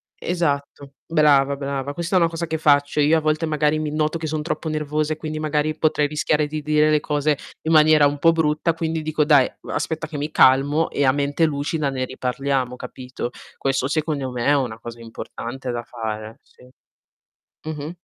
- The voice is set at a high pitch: No, medium, 150 Hz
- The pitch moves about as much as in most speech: No, narrow, 2.1 semitones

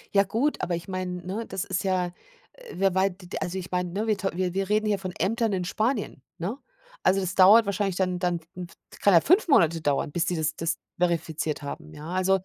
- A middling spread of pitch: No, narrow, 2.3 semitones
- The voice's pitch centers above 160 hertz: Yes, medium, 185 Hz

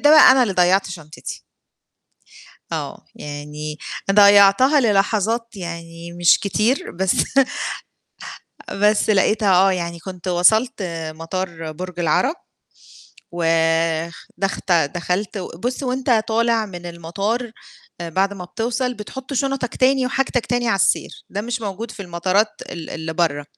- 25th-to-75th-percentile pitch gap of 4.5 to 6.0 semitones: Yes, average, 5.2 semitones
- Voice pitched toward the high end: Yes, high, 195 Hz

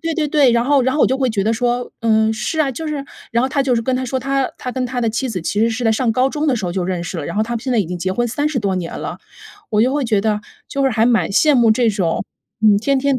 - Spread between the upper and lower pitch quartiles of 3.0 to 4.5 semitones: Yes, average, 3.6 semitones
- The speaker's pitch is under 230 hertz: No, high, 240 Hz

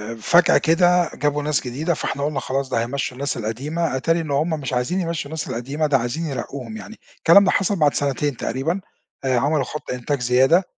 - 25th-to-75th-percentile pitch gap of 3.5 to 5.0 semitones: Yes, average, 4.1 semitones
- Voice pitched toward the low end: No, medium, 145 Hz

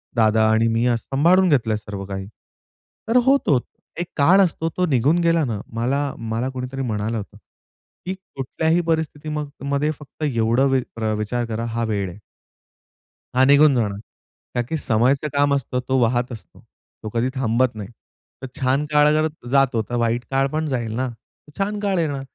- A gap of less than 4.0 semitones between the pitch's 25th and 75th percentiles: No, average, 4.7 semitones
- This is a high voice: No, low, 130 Hz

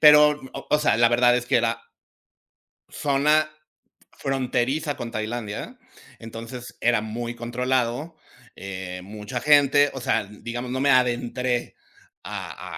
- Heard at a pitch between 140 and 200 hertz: No, low, 120 Hz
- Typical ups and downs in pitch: Yes, average, 3.1 semitones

